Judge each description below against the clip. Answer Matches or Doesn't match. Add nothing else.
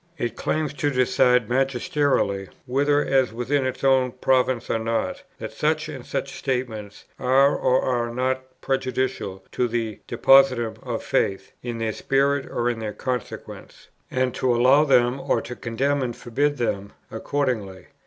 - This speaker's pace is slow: Doesn't match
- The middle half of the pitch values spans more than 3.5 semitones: Doesn't match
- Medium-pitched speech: Doesn't match